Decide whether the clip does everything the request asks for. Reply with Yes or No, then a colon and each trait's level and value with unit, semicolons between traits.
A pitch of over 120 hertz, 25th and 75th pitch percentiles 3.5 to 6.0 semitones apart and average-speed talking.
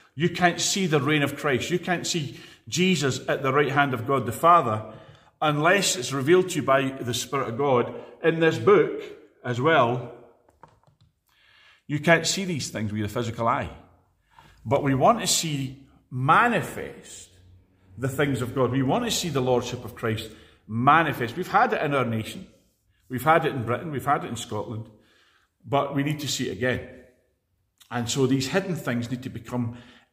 Yes: low, 135 Hz; average, 5.0 semitones; average, 185 wpm